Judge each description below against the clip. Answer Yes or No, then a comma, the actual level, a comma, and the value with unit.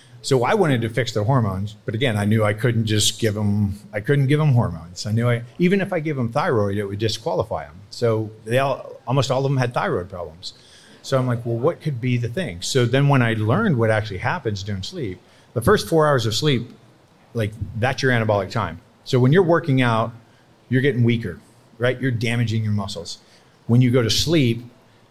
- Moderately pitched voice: No, low, 120 Hz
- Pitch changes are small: No, average, 3.4 semitones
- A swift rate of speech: Yes, fast, 220 wpm